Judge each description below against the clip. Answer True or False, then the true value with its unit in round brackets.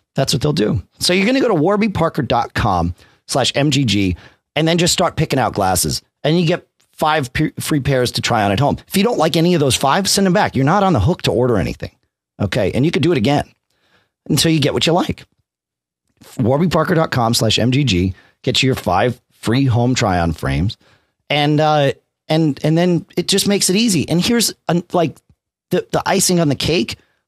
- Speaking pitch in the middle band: True (145 Hz)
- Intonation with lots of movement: True (5.9 semitones)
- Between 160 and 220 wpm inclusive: True (200 wpm)